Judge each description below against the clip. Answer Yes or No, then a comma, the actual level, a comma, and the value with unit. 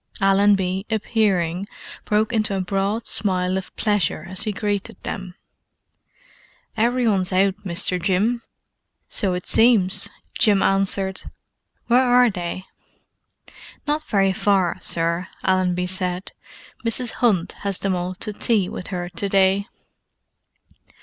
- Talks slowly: Yes, slow, 125 wpm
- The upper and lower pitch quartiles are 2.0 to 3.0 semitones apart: Yes, narrow, 2.5 semitones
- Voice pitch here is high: Yes, high, 195 Hz